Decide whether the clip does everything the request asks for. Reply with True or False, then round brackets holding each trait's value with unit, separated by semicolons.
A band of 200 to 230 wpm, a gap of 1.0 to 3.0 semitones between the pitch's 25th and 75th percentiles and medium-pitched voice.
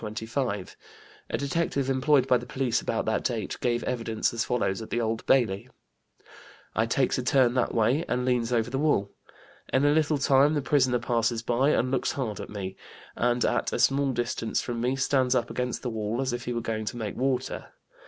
False (205 wpm; 2.7 semitones; 125 Hz)